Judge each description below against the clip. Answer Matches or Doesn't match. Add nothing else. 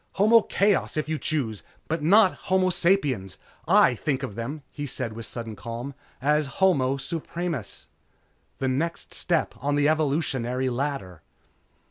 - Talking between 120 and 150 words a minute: Matches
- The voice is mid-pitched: Matches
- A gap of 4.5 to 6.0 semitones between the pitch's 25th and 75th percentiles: Matches